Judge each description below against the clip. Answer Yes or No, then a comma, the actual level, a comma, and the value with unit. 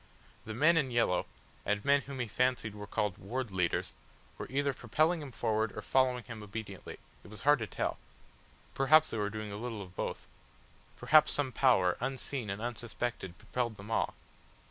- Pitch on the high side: No, low, 115 Hz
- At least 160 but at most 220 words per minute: Yes, average, 180 wpm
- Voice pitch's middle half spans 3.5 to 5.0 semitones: Yes, average, 4.2 semitones